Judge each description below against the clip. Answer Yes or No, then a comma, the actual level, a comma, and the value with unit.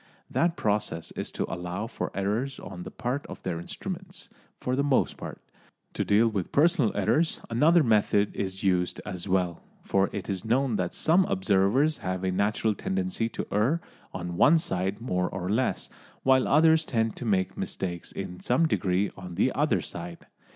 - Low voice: Yes, low, 105 Hz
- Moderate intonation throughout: No, wide, 6.3 semitones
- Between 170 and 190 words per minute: Yes, average, 175 wpm